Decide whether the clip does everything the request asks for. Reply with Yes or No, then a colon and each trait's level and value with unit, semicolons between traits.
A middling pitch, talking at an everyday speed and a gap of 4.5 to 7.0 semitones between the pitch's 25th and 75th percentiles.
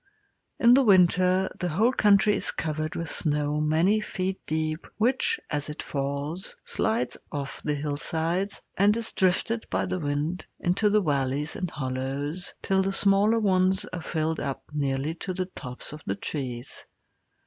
Yes: medium, 170 Hz; average, 160 wpm; average, 4.8 semitones